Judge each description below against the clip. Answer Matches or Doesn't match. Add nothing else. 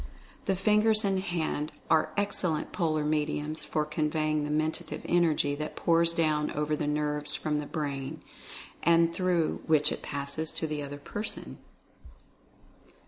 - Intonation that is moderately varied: Doesn't match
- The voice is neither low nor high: Matches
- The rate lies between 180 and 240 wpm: Doesn't match